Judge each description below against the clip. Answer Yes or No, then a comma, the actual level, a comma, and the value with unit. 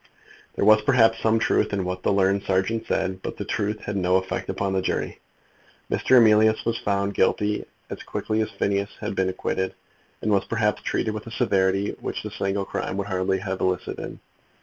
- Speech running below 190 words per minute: No, average, 195 wpm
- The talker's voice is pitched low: Yes, low, 100 Hz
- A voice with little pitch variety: Yes, narrow, 2.3 semitones